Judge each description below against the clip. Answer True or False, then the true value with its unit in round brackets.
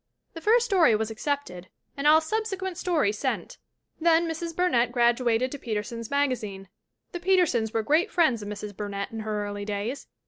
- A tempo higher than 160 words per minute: True (175 wpm)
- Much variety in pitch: True (7.7 semitones)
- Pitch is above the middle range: True (250 Hz)